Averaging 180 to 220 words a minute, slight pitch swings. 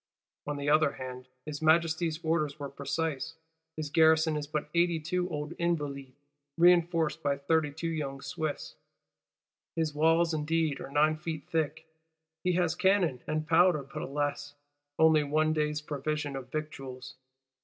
No: average, 145 wpm; narrow, 2.1 semitones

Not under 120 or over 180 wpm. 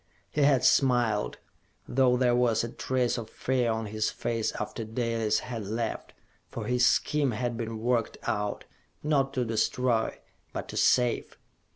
Yes: average, 155 wpm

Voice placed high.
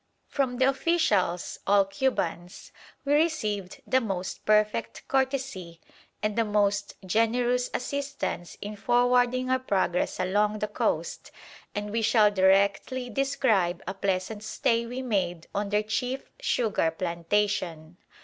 Yes: high, 210 Hz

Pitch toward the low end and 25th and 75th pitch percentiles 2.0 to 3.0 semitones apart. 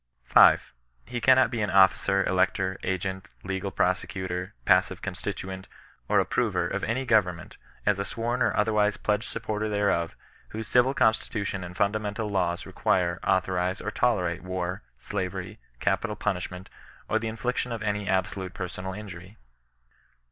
Yes: low, 100 Hz; average, 2.7 semitones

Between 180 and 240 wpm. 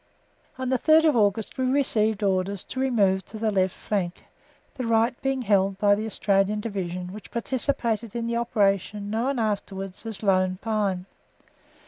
No: average, 160 wpm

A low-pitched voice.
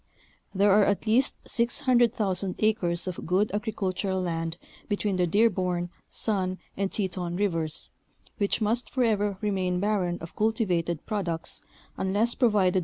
No: high, 195 Hz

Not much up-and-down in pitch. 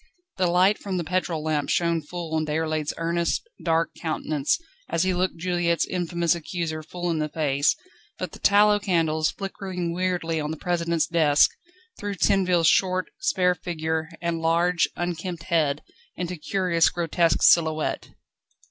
Yes: narrow, 2.2 semitones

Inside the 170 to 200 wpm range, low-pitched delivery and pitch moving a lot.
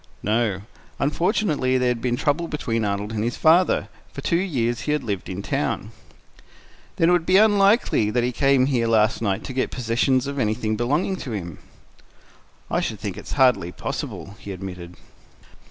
Yes: average, 175 wpm; low, 125 Hz; wide, 5.8 semitones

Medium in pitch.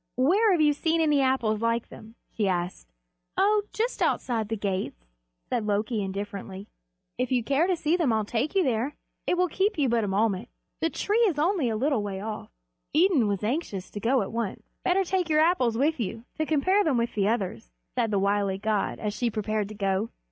No: high, 235 Hz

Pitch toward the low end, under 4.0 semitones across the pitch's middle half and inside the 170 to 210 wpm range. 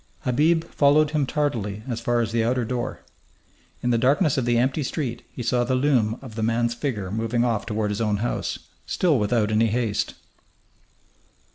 Yes: low, 120 Hz; average, 2.9 semitones; average, 180 wpm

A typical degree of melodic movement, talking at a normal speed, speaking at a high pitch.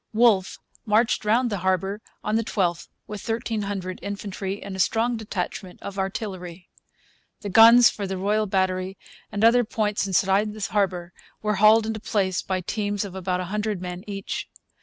No: narrow, 2.3 semitones; average, 165 wpm; high, 200 Hz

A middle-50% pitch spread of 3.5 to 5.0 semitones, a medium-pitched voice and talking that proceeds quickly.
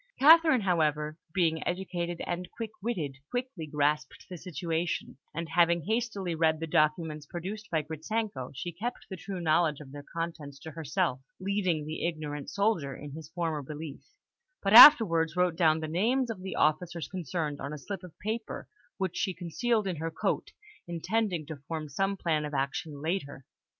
No: average, 3.8 semitones; medium, 165 Hz; average, 170 wpm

